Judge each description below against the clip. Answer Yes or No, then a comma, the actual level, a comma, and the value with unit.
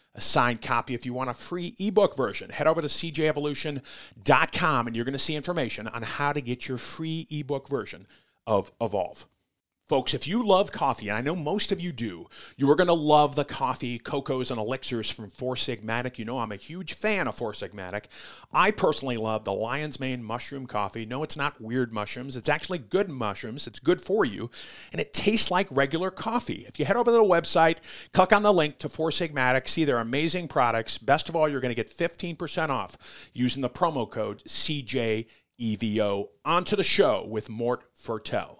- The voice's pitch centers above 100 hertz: Yes, medium, 140 Hz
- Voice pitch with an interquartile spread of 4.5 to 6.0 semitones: Yes, wide, 5.4 semitones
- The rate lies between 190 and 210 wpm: Yes, average, 200 wpm